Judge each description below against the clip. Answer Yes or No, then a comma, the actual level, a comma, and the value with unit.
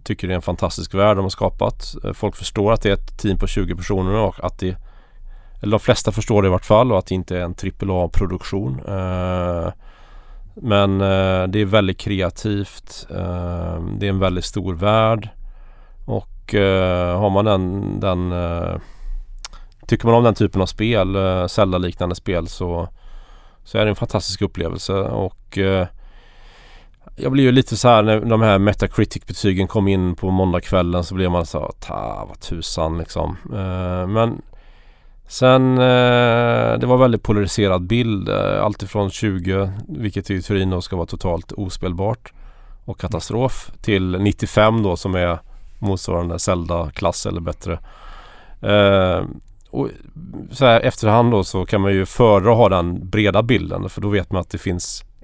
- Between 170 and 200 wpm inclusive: No, average, 155 wpm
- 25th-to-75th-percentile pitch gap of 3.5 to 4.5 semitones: No, average, 2.8 semitones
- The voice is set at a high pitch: No, very low, 95 Hz